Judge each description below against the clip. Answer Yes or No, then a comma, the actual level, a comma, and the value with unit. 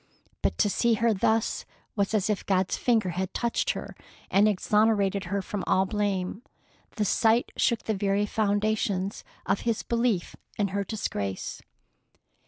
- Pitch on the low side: No, high, 205 Hz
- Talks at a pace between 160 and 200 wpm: No, average, 150 wpm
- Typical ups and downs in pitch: No, narrow, 2.3 semitones